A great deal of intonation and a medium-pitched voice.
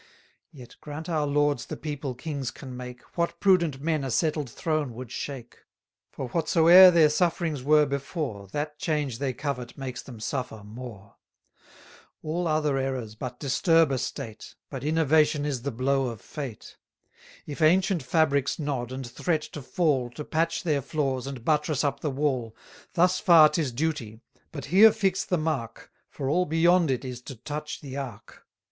No: average, 3.8 semitones; medium, 145 Hz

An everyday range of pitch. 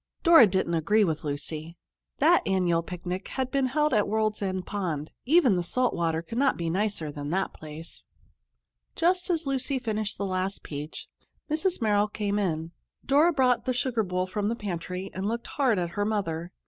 No: wide, 6.5 semitones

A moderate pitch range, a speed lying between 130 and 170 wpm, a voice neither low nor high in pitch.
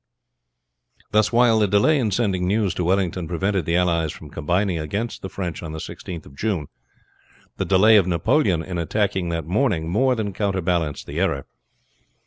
No: average, 3.9 semitones; average, 165 wpm; very low, 95 Hz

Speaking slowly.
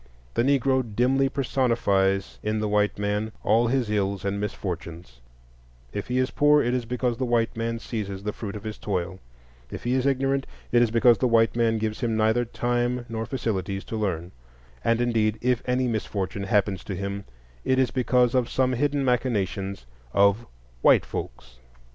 No: average, 180 wpm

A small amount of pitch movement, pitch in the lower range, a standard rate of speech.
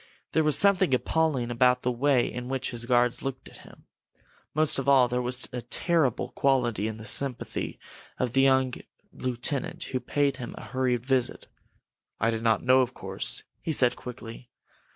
Yes: narrow, 2.0 semitones; low, 125 Hz; average, 175 wpm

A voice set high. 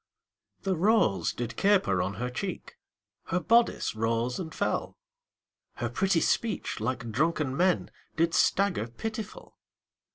No: medium, 165 Hz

